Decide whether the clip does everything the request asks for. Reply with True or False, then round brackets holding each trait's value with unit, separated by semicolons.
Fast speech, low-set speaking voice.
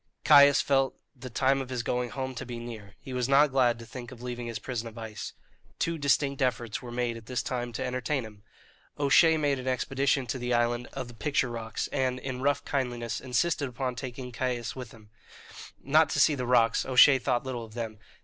True (215 wpm; 125 Hz)